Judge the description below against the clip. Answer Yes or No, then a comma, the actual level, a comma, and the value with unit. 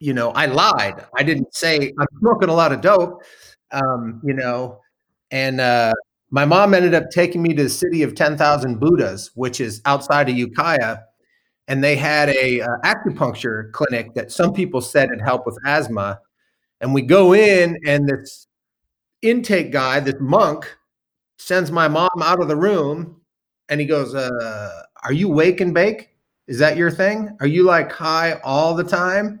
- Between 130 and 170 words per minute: No, average, 180 wpm